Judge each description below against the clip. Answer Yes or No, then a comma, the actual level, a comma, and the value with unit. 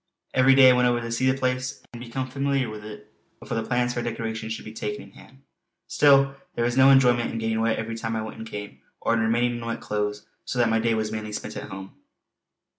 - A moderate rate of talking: No, fast, 250 wpm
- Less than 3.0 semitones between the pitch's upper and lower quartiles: Yes, narrow, 2.5 semitones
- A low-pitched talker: Yes, low, 115 Hz